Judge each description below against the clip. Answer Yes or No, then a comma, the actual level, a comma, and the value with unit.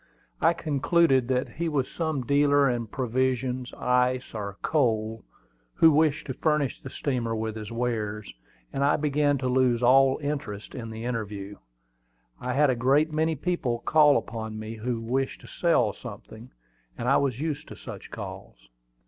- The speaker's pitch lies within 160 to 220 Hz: No, low, 130 Hz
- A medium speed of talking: Yes, average, 165 wpm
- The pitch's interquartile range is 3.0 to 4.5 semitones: Yes, average, 4.1 semitones